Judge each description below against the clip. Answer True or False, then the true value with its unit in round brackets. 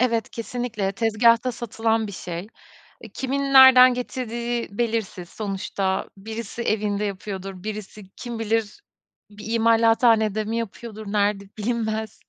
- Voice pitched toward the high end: True (220 Hz)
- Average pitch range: False (2.2 semitones)